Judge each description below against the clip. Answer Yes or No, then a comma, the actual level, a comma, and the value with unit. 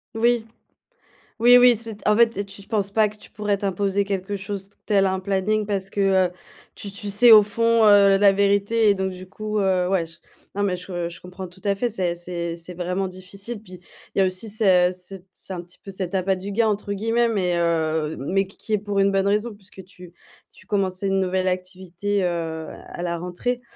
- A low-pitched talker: No, high, 195 Hz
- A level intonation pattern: Yes, narrow, 2.2 semitones